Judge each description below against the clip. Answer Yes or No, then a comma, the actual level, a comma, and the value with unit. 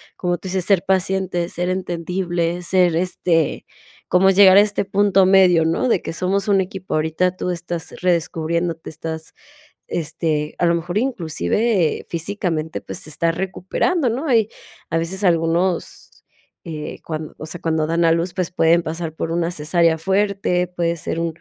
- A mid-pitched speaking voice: Yes, medium, 175 Hz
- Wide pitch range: No, narrow, 2.5 semitones